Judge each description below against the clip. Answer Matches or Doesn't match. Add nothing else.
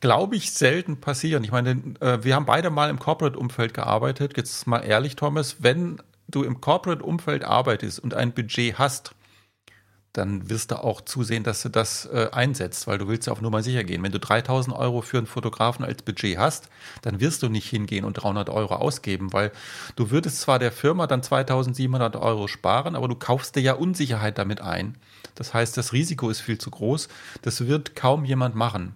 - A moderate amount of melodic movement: Matches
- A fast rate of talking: Matches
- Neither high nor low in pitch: Doesn't match